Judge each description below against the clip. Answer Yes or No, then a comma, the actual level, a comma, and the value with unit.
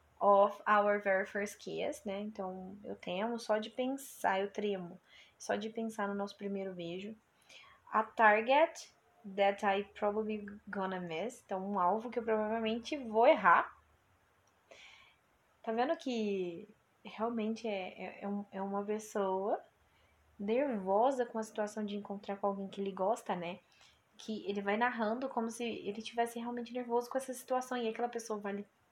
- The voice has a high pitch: Yes, high, 210 Hz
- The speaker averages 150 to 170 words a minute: Yes, average, 155 wpm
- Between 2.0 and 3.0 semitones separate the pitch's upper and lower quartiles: Yes, average, 2.7 semitones